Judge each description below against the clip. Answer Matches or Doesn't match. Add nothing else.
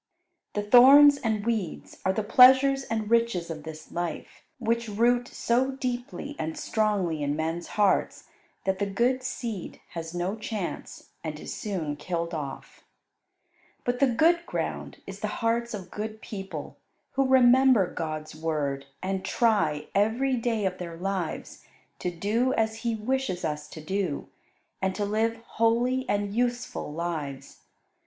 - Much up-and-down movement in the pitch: Matches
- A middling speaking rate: Matches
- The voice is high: Matches